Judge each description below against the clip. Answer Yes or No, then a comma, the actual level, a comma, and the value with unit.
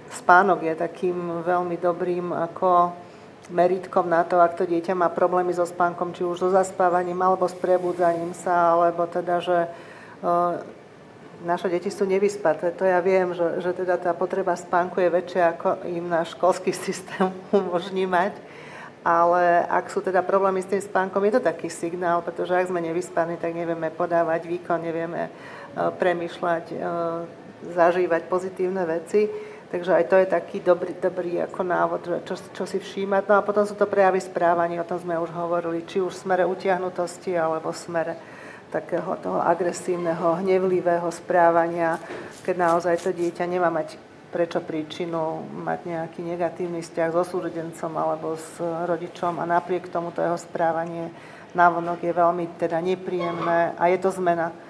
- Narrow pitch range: Yes, narrow, 1.3 semitones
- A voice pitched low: No, medium, 175 Hz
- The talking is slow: No, average, 160 wpm